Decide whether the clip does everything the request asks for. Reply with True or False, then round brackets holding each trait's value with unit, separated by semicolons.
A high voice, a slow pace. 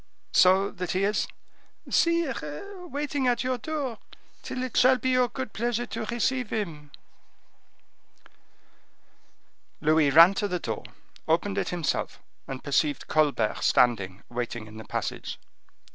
True (200 Hz; 130 wpm)